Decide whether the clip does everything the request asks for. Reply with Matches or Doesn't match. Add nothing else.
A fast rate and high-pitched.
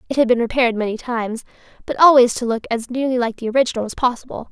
Matches